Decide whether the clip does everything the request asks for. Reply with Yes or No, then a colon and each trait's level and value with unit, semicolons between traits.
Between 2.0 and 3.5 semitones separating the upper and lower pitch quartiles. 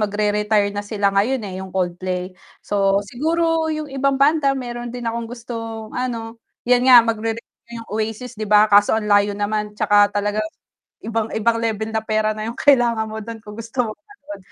Yes: narrow, 2.6 semitones